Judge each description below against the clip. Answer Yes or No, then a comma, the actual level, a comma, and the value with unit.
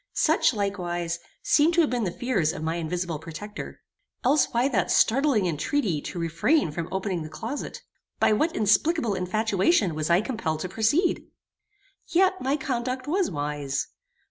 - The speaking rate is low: No, average, 155 wpm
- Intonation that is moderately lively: No, wide, 7.9 semitones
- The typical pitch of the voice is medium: No, high, 205 Hz